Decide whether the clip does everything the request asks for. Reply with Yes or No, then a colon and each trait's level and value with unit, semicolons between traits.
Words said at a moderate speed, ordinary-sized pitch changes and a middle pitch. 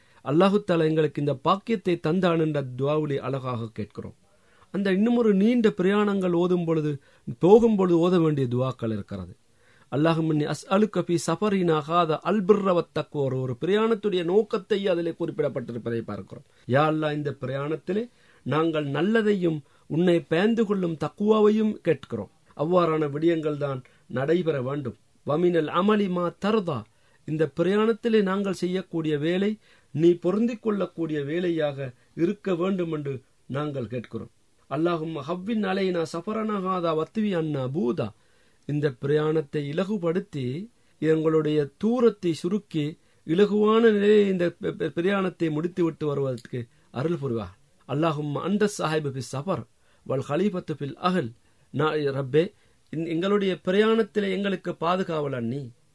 Yes: average, 100 wpm; average, 5.0 semitones; medium, 160 Hz